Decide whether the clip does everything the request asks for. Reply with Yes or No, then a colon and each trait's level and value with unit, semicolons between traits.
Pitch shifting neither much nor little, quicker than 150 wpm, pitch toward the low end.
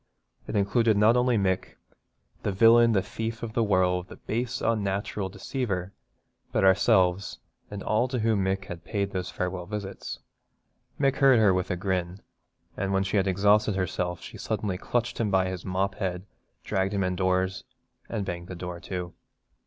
Yes: average, 3.0 semitones; average, 170 wpm; very low, 95 Hz